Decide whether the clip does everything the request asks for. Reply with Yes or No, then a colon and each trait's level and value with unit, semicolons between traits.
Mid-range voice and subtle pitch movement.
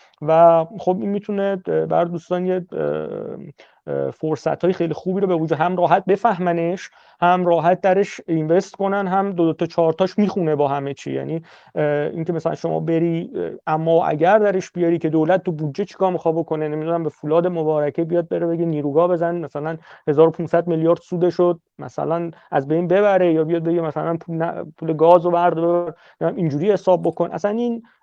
Yes: medium, 170 Hz; narrow, 1.9 semitones